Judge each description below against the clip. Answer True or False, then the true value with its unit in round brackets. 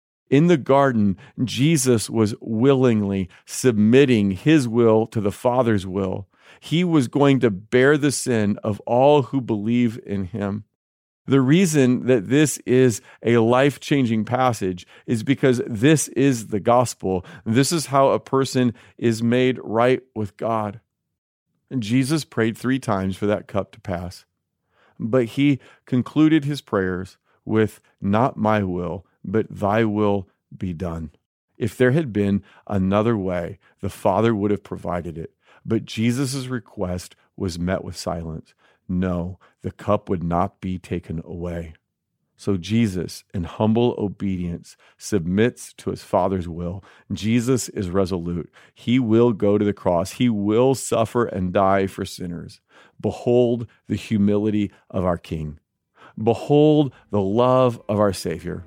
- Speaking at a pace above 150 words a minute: False (145 wpm)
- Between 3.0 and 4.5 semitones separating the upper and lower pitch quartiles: False (4.9 semitones)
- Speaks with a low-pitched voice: True (110 Hz)